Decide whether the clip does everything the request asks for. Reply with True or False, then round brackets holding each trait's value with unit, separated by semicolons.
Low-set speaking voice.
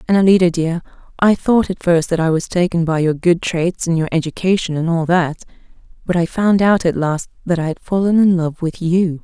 False (175 Hz)